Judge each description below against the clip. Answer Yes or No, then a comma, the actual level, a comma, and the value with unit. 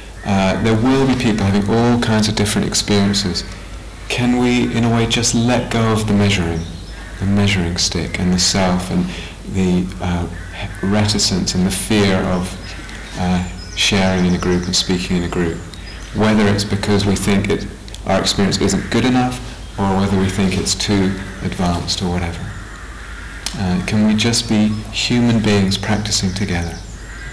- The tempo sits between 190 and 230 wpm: No, average, 165 wpm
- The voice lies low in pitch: Yes, very low, 95 Hz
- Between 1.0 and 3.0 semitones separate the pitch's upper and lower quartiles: Yes, average, 2.7 semitones